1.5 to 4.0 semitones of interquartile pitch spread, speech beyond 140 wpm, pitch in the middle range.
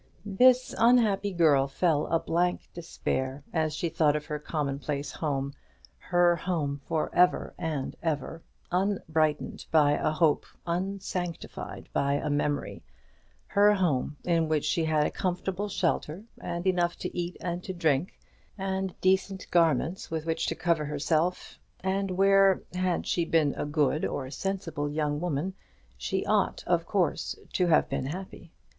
Yes: average, 3.6 semitones; average, 150 wpm; medium, 165 Hz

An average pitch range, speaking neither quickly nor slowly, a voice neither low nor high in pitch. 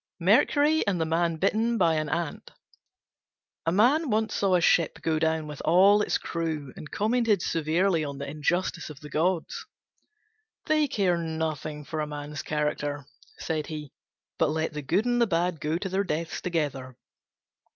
Yes: average, 4.3 semitones; average, 170 wpm; medium, 165 Hz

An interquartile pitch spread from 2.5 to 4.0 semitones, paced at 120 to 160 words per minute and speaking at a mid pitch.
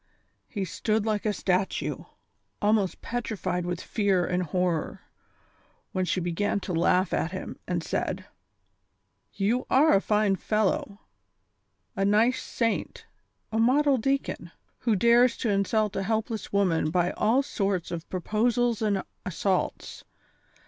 No: average, 3.5 semitones; slow, 135 wpm; high, 205 Hz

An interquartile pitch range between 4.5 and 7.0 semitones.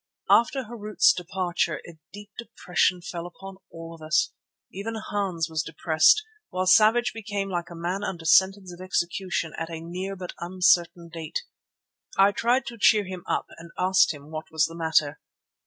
No: average, 3.4 semitones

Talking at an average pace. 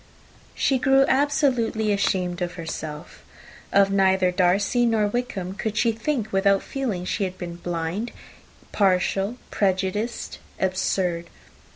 No: slow, 125 wpm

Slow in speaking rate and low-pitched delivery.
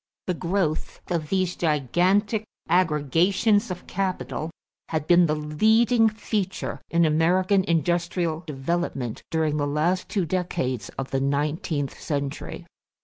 No: slow, 120 wpm; medium, 170 Hz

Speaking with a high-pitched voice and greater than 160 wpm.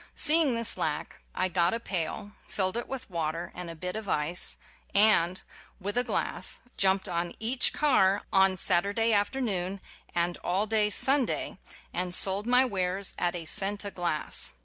Yes: high, 195 Hz; average, 170 wpm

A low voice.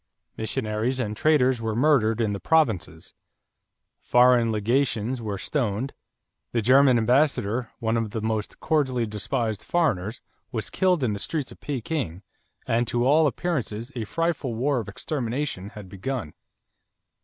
Yes: low, 120 Hz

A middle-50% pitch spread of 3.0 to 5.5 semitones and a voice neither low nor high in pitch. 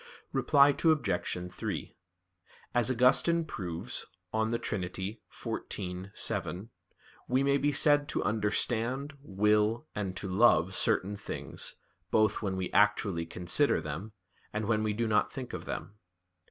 No: average, 4.8 semitones; low, 105 Hz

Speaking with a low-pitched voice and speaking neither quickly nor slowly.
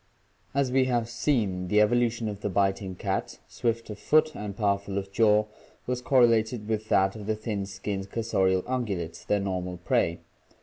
Yes: low, 105 Hz; average, 170 wpm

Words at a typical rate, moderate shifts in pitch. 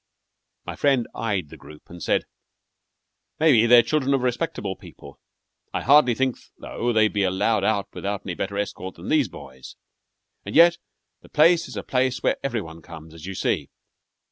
No: average, 175 wpm; wide, 6.0 semitones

